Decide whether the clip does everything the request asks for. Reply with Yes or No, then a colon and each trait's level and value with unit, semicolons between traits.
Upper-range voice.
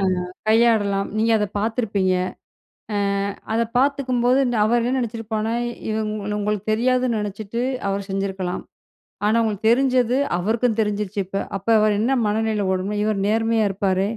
Yes: high, 215 Hz